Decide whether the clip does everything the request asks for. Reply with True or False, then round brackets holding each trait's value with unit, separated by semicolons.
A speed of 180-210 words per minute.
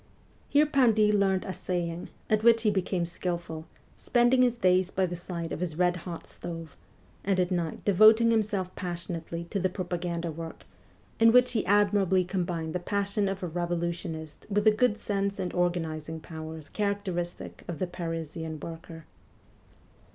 False (155 wpm)